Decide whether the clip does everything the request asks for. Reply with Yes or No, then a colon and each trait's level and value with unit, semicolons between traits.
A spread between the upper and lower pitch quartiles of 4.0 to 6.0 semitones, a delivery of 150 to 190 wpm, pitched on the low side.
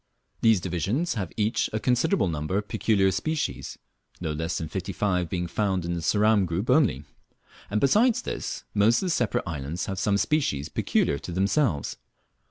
Yes: average, 4.9 semitones; average, 175 wpm; very low, 95 Hz